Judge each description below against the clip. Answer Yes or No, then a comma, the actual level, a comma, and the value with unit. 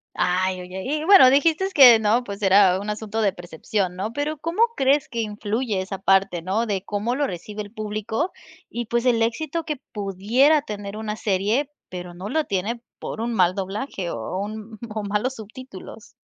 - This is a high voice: Yes, high, 215 Hz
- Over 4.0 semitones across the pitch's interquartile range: Yes, average, 4.7 semitones